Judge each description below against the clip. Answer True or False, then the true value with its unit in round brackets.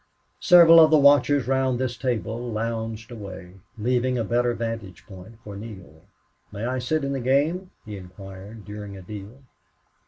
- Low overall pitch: True (115 Hz)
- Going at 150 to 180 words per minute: True (160 wpm)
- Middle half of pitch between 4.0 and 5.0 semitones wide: True (4.3 semitones)